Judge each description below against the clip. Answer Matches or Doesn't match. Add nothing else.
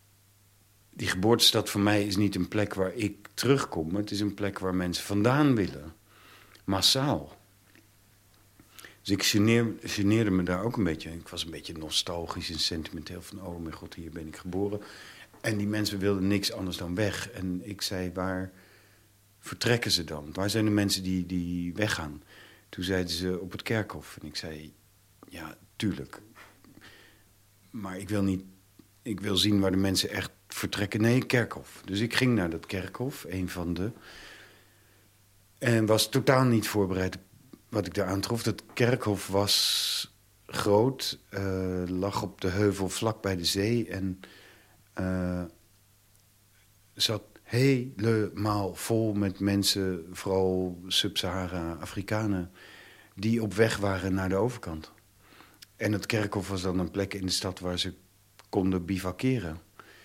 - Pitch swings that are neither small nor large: Doesn't match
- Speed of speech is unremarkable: Matches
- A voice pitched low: Matches